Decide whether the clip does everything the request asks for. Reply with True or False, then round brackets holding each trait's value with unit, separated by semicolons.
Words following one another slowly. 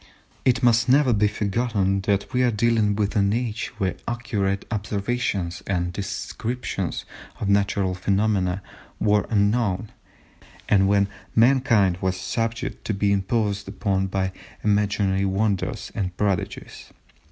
True (125 wpm)